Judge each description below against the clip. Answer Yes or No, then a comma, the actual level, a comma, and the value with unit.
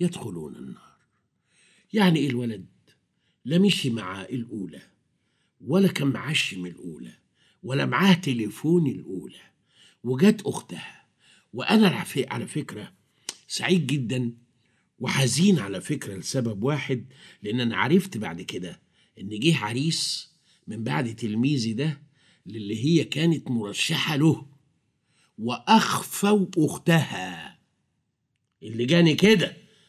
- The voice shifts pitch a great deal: Yes, wide, 6.4 semitones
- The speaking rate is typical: Yes, average, 105 wpm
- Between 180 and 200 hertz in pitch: No, medium, 145 Hz